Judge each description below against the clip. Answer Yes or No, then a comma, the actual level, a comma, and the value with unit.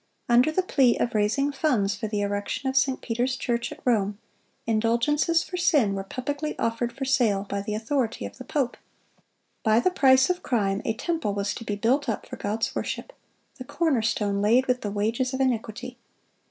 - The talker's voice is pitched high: Yes, high, 235 Hz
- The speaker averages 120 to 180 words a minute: No, average, 190 wpm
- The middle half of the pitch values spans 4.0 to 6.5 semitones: Yes, average, 4.4 semitones